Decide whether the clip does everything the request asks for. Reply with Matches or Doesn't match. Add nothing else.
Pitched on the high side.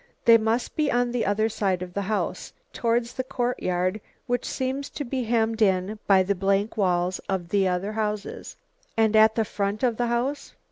Matches